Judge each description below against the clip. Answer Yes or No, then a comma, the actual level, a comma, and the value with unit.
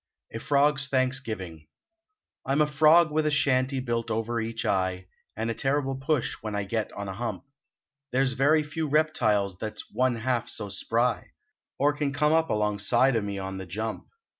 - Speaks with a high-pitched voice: No, low, 125 Hz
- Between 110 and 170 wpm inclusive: No, average, 195 wpm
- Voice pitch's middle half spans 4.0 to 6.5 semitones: Yes, average, 5.0 semitones